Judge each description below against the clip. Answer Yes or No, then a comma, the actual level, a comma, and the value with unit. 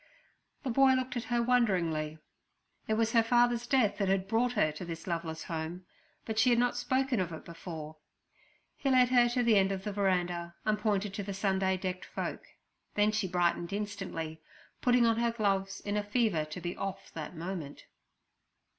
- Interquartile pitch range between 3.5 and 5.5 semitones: Yes, average, 5.1 semitones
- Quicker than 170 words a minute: Yes, average, 190 wpm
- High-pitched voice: Yes, high, 200 Hz